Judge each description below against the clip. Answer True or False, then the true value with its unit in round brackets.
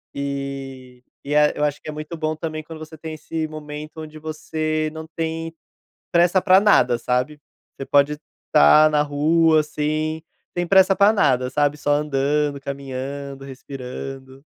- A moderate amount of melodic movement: False (2.3 semitones)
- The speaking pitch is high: False (150 Hz)